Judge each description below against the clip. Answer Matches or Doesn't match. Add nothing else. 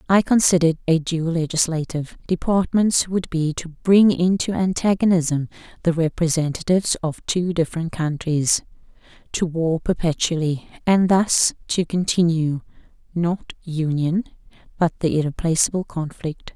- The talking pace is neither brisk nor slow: Doesn't match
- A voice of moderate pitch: Matches